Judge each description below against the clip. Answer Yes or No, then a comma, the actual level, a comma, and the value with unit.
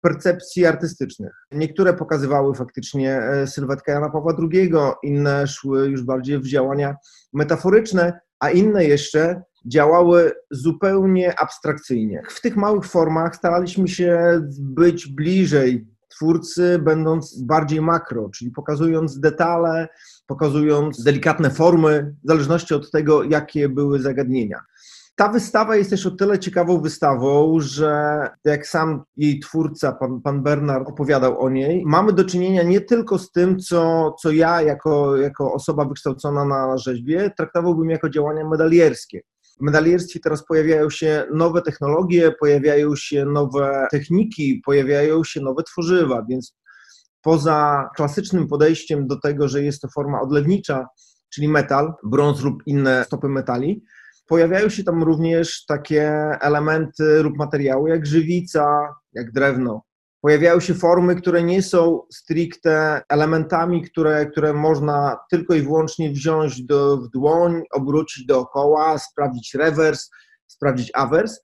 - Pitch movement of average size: Yes, average, 3.0 semitones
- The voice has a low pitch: No, medium, 155 Hz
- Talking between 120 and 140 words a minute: Yes, average, 130 wpm